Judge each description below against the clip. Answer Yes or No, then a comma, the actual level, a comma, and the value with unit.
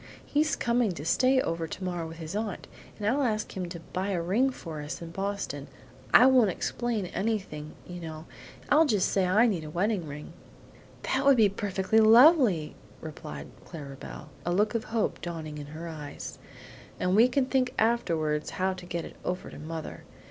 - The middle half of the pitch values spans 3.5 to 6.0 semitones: Yes, wide, 5.6 semitones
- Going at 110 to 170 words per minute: No, average, 185 wpm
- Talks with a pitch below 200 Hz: Yes, medium, 185 Hz